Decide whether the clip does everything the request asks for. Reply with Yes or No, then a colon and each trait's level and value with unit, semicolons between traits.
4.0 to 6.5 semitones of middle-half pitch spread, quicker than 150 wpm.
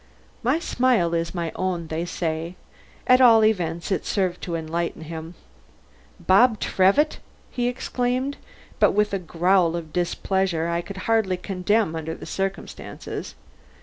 No: average, 4.6 semitones; average, 140 wpm